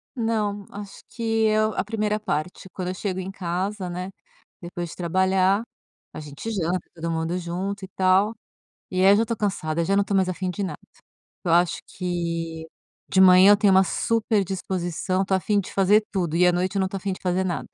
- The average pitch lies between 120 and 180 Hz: No, high, 190 Hz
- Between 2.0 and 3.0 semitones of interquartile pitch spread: Yes, narrow, 2.4 semitones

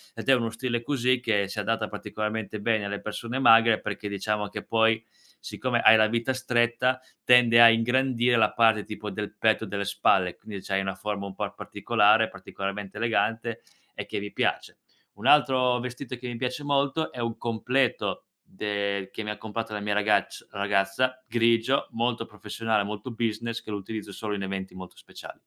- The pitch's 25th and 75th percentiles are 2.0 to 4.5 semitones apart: Yes, average, 2.7 semitones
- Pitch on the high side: No, low, 115 Hz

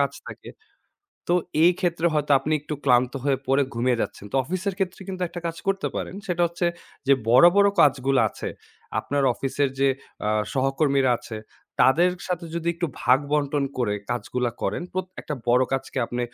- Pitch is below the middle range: No, medium, 145 Hz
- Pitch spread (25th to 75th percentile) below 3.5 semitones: No, average, 4.8 semitones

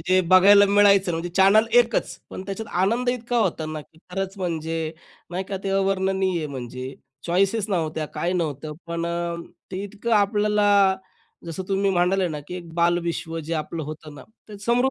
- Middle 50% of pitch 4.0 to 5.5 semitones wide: No, average, 3.4 semitones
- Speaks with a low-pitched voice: No, high, 190 Hz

